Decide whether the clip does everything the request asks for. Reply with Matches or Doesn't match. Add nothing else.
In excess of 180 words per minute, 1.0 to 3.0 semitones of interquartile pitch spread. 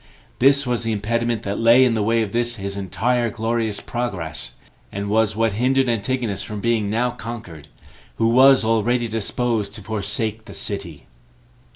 Doesn't match